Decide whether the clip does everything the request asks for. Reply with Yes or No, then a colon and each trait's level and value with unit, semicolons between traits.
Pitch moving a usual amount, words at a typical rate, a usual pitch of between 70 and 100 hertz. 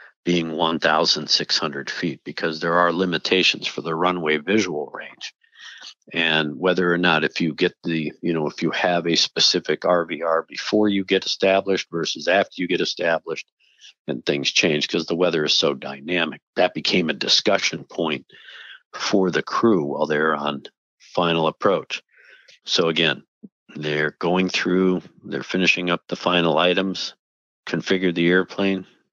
No: narrow, 2.1 semitones; average, 150 wpm; very low, 90 Hz